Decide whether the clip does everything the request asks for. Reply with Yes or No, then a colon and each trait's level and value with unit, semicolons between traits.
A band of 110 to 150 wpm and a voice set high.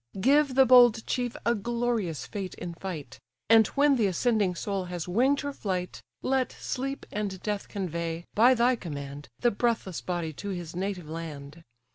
No: average, 165 wpm; high, 200 Hz